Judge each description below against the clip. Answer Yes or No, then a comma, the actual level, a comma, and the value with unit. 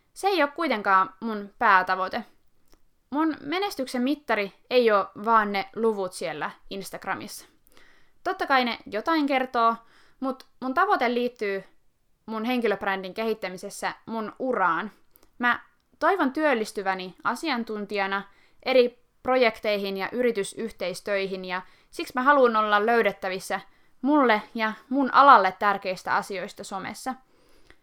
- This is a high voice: Yes, high, 225 Hz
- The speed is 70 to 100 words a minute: No, average, 110 wpm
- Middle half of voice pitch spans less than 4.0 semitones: No, average, 4.9 semitones